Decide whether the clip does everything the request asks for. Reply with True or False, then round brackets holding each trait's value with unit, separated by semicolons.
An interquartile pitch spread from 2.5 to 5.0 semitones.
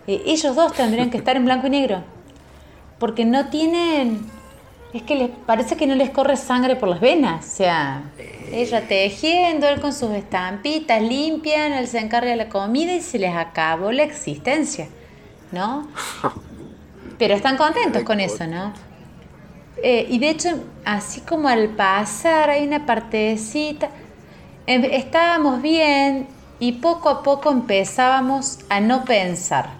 False (5.6 semitones)